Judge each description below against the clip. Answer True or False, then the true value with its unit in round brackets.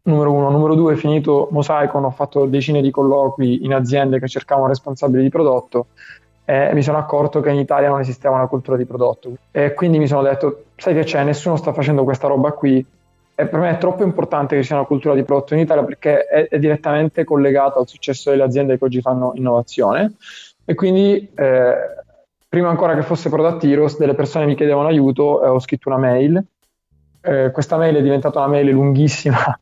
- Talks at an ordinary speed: False (205 wpm)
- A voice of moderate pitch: True (145 Hz)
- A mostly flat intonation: True (2.1 semitones)